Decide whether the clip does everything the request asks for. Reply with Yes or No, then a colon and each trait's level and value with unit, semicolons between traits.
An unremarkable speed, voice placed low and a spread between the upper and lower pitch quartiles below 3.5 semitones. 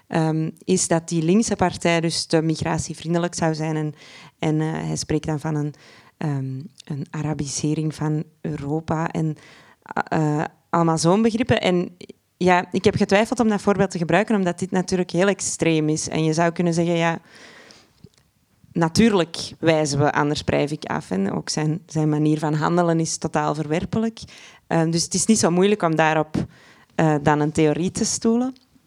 No: average, 175 wpm; medium, 165 Hz; average, 2.8 semitones